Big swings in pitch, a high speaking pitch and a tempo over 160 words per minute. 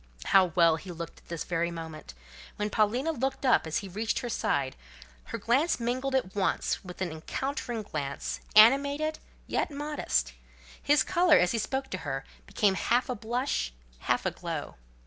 Yes: wide, 7.9 semitones; high, 215 Hz; average, 170 wpm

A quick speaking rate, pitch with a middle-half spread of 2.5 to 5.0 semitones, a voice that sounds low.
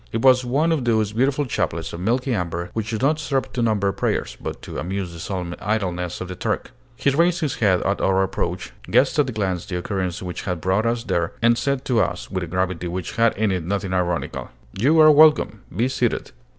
No: fast, 225 wpm; wide, 5.6 semitones; low, 105 Hz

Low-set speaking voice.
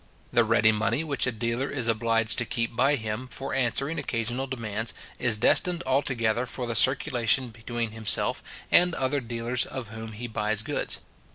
Yes: low, 120 Hz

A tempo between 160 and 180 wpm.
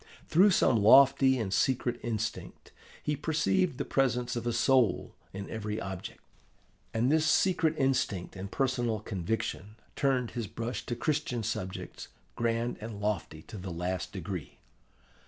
No: average, 140 wpm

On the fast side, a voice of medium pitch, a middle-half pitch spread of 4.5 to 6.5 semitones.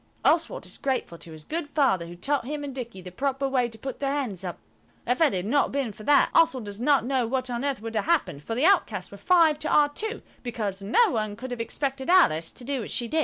No: fast, 260 wpm; very high, 260 Hz; average, 5.1 semitones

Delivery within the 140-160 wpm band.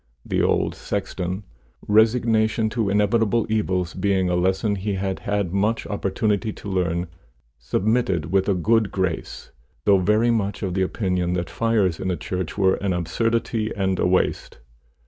Yes: average, 150 wpm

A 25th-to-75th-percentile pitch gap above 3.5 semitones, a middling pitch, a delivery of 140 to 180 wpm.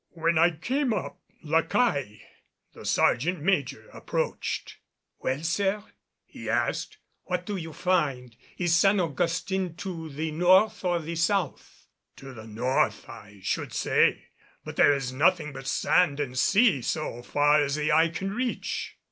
Yes: average, 4.7 semitones; medium, 165 Hz; average, 150 wpm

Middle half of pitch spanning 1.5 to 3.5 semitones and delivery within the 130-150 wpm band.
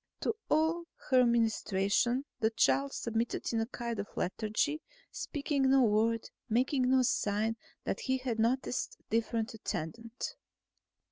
Yes: average, 2.9 semitones; slow, 135 wpm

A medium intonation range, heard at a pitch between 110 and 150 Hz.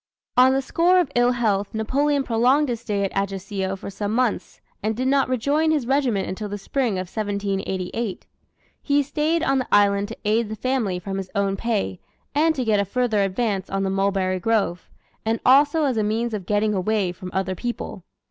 No: average, 4.6 semitones; high, 220 Hz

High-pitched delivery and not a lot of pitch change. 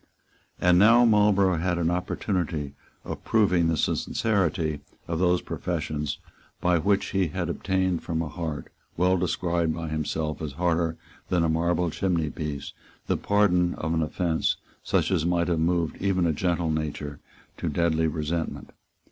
No: very low, 85 Hz; narrow, 2.3 semitones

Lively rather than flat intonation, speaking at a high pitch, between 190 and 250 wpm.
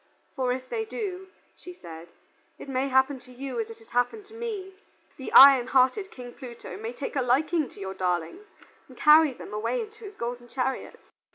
Yes: wide, 7.8 semitones; very high, 265 Hz; average, 195 wpm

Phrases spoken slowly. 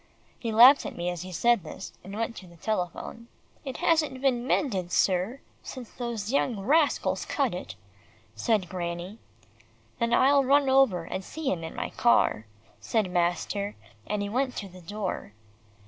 No: average, 165 wpm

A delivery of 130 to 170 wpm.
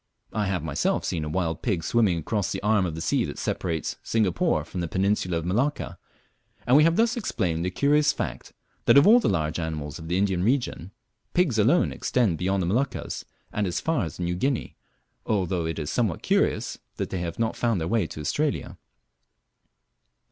No: average, 195 wpm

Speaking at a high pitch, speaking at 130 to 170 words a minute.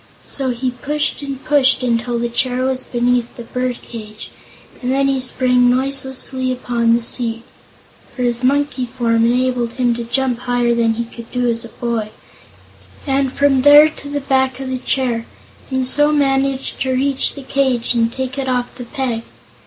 No: very high, 255 Hz; average, 180 wpm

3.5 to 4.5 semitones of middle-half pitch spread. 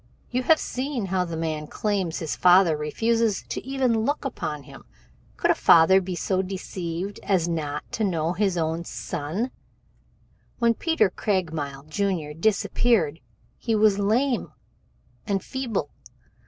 No: wide, 5.6 semitones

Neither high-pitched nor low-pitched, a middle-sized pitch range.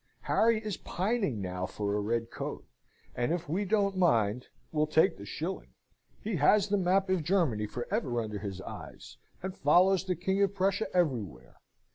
No: medium, 175 Hz; wide, 8.8 semitones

